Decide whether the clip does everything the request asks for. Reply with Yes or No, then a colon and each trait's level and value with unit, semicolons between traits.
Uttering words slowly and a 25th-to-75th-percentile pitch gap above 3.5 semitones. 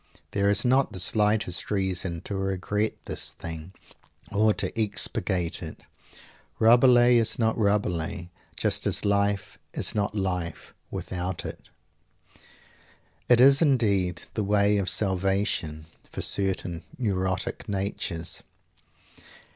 No: slow, 115 wpm; average, 2.8 semitones